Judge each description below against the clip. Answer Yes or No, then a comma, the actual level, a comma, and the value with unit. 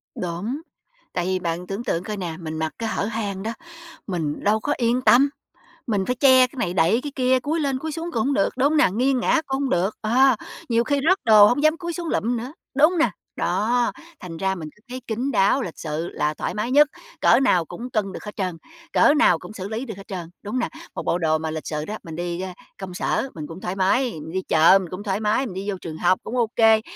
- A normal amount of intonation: No, wide, 6.2 semitones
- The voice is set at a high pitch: Yes, high, 215 Hz